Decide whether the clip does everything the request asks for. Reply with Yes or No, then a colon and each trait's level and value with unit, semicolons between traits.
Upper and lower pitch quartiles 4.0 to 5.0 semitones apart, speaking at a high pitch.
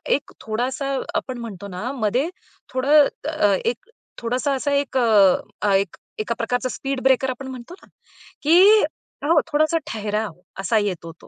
Yes: average, 4.4 semitones; high, 245 Hz